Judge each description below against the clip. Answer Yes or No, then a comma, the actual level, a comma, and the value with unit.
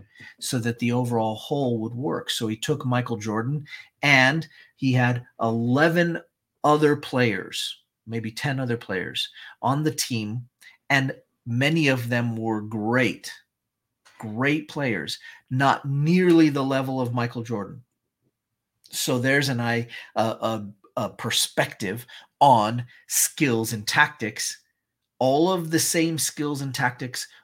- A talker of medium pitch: No, low, 125 Hz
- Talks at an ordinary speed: No, slow, 125 wpm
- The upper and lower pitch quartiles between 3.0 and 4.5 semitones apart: Yes, average, 3.9 semitones